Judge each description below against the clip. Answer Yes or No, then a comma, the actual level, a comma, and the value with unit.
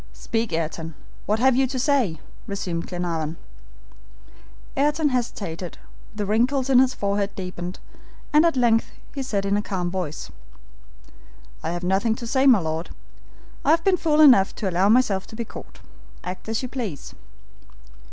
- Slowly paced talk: No, average, 155 wpm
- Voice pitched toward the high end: Yes, high, 210 Hz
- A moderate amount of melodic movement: No, wide, 6.3 semitones